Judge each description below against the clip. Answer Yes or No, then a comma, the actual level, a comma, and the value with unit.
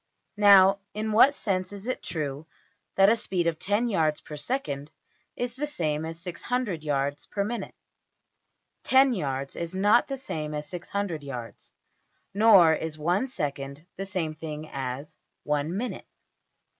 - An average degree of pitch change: No, wide, 5.7 semitones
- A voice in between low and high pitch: Yes, medium, 170 Hz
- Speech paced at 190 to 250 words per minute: No, average, 140 wpm